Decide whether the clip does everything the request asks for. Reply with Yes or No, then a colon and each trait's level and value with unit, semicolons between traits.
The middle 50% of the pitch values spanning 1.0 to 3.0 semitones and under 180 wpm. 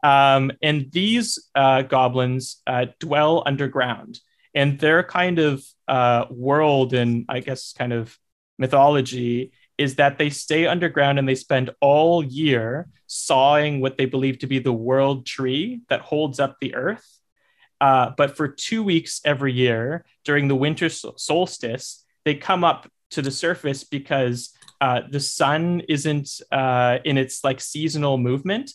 Yes: narrow, 2.6 semitones; average, 150 wpm